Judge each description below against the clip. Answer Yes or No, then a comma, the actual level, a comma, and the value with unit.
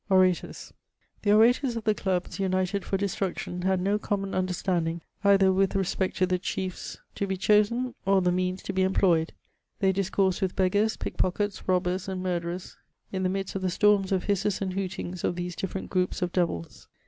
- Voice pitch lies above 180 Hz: Yes, high, 190 Hz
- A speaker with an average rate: Yes, average, 185 wpm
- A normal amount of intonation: No, narrow, 1.4 semitones